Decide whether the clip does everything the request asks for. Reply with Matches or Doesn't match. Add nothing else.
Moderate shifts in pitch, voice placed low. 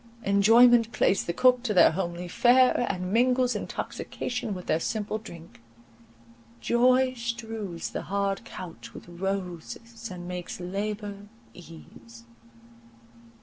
Doesn't match